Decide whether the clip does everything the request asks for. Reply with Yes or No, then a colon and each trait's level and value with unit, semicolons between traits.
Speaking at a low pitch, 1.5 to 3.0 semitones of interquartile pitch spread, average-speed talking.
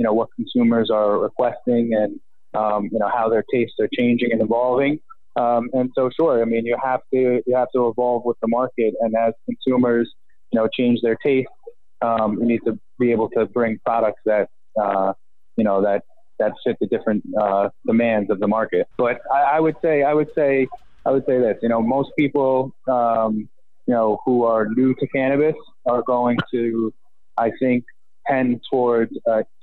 Yes: low, 120 Hz; narrow, 2.5 semitones; average, 195 wpm